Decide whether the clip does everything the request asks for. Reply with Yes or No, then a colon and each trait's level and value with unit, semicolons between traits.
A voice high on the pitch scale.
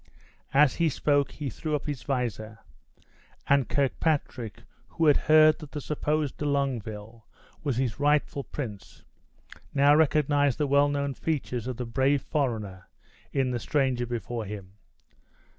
No: medium, 140 Hz